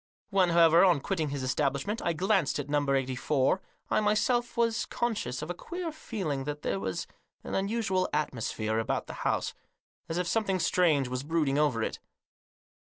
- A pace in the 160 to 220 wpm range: Yes, average, 175 wpm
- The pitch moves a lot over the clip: Yes, wide, 6.1 semitones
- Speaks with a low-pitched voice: No, medium, 165 Hz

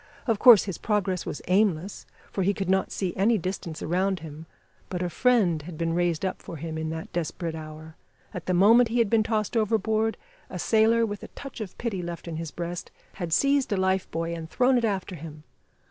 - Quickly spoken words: Yes, fast, 215 wpm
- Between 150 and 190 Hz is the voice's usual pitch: Yes, medium, 185 Hz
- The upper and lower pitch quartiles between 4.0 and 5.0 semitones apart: Yes, average, 4.6 semitones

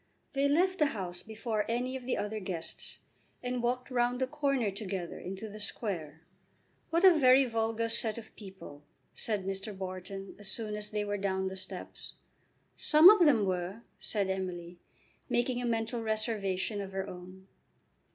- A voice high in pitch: Yes, high, 215 Hz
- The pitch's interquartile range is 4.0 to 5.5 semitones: Yes, average, 4.3 semitones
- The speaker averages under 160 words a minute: No, average, 165 wpm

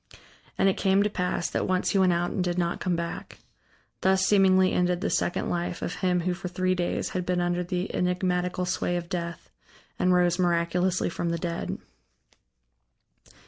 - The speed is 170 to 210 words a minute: Yes, average, 185 wpm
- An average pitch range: No, narrow, 1.0 semitones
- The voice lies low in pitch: No, medium, 180 Hz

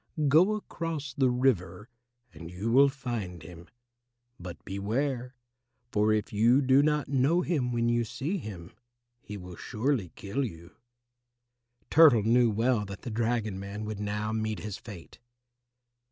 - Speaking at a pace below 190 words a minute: Yes, average, 145 wpm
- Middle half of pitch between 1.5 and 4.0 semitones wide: No, average, 4.8 semitones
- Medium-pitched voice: No, low, 115 Hz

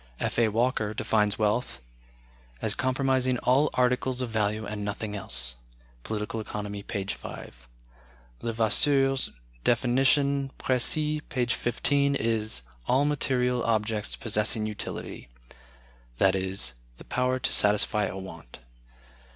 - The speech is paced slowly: Yes, slow, 110 wpm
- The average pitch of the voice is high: No, low, 115 Hz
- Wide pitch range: No, average, 3.7 semitones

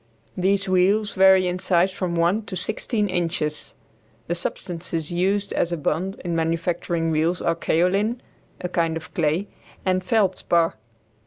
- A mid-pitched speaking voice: Yes, medium, 180 Hz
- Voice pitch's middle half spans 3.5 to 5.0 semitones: No, narrow, 2.4 semitones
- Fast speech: No, average, 145 wpm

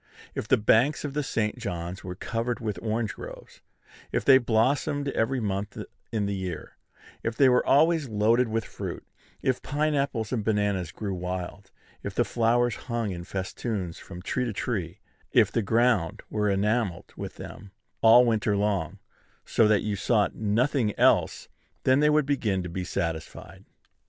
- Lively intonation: No, average, 4.0 semitones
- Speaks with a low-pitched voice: Yes, low, 110 Hz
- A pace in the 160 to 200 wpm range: Yes, average, 165 wpm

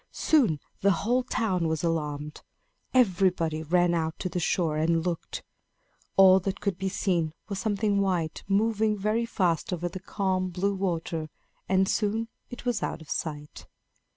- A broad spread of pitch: No, average, 3.5 semitones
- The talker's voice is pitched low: No, medium, 185 Hz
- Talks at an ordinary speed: Yes, average, 155 wpm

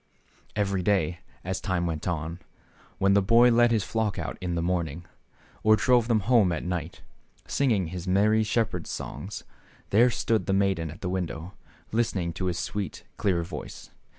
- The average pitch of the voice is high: No, very low, 95 Hz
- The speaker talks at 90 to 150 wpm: No, average, 165 wpm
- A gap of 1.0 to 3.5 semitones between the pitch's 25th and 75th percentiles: No, average, 3.9 semitones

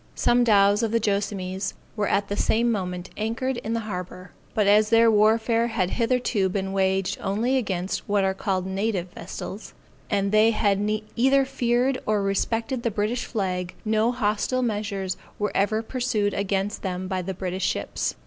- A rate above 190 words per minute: No, average, 170 wpm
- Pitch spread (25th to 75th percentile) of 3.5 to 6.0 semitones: No, average, 3.0 semitones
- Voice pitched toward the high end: Yes, high, 205 Hz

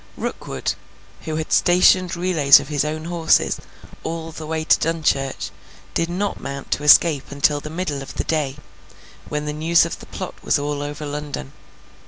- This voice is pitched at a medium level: Yes, medium, 155 Hz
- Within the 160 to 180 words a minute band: Yes, average, 175 wpm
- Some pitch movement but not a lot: No, narrow, 2.3 semitones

